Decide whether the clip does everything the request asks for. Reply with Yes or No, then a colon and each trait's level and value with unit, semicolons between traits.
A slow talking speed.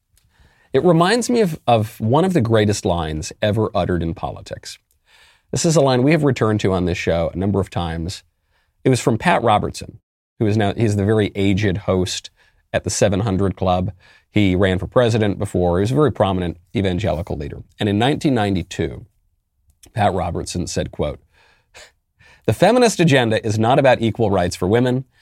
No: average, 180 wpm